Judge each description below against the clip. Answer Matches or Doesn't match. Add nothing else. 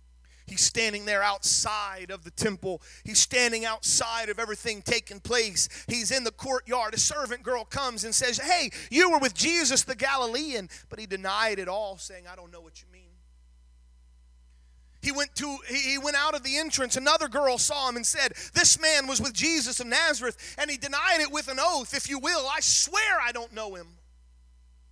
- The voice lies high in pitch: Matches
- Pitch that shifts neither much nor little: Doesn't match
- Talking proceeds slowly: Doesn't match